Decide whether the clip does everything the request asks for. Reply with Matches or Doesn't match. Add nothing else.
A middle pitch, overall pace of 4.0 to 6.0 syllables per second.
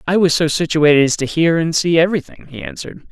Doesn't match